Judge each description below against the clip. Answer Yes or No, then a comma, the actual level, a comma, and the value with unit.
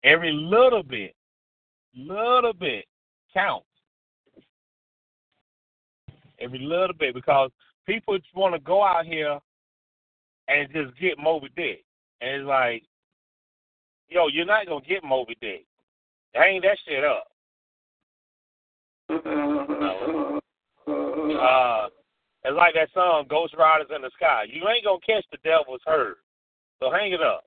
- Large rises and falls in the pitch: Yes, wide, 6.3 semitones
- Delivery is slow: Yes, slow, 130 wpm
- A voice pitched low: No, medium, 160 Hz